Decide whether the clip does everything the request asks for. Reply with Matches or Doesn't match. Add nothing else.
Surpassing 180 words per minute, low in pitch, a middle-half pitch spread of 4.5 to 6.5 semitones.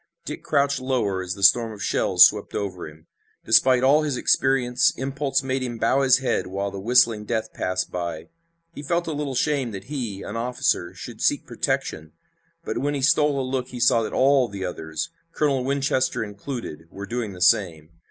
Matches